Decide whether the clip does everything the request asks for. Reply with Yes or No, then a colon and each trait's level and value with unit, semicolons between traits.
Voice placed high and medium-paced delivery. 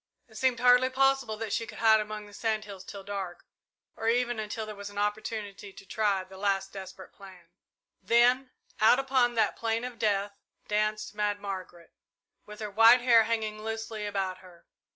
Yes: high, 215 Hz; average, 180 wpm